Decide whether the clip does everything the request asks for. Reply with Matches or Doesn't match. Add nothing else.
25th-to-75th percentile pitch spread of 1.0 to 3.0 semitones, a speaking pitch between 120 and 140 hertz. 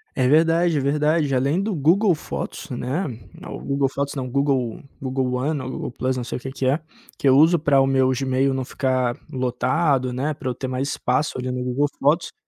Matches